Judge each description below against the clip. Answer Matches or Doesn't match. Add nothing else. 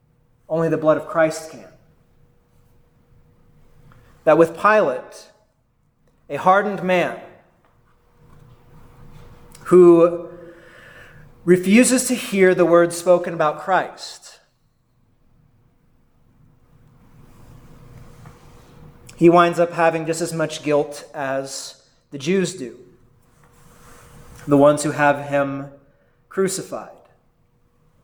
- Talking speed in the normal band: Doesn't match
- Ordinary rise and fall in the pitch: Matches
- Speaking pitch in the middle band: Matches